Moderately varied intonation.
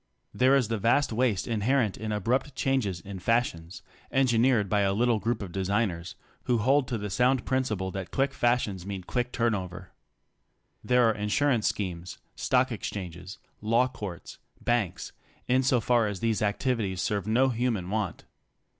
Yes: average, 4.2 semitones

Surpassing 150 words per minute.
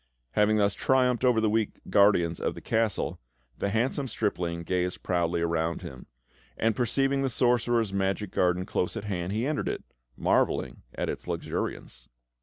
Yes: average, 160 wpm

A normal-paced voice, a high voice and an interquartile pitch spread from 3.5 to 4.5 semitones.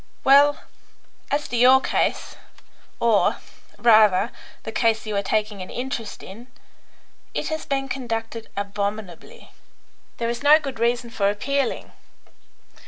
No: slow, 125 wpm; high, 230 Hz; average, 4.0 semitones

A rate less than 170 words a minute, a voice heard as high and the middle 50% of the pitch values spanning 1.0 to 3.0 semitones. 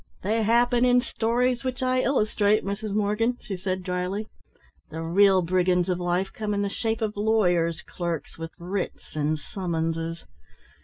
No: average, 155 wpm; high, 200 Hz; average, 4.0 semitones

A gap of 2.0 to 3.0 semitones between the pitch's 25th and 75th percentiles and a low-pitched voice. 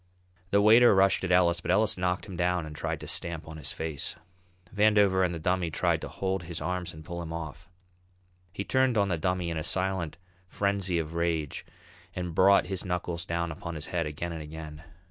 Yes: narrow, 2.5 semitones; very low, 85 Hz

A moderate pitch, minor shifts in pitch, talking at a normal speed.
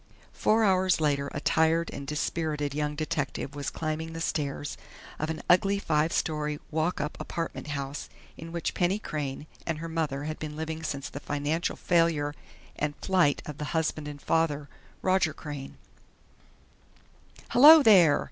Yes: medium, 155 Hz; narrow, 2.2 semitones; average, 155 wpm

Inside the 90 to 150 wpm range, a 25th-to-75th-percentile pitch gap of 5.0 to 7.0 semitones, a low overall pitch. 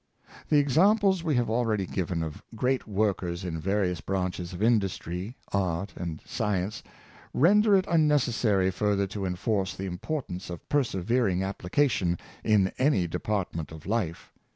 Yes: average, 140 wpm; wide, 5.4 semitones; low, 100 Hz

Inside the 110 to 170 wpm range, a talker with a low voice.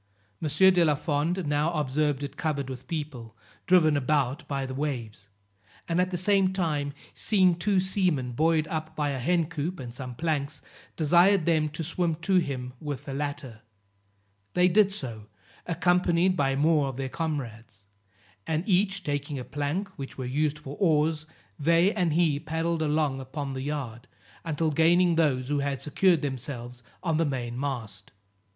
No: average, 165 wpm; medium, 150 Hz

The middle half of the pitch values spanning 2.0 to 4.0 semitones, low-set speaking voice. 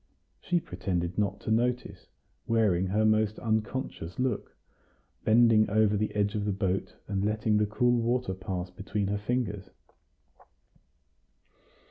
Yes: narrow, 2.6 semitones; low, 105 Hz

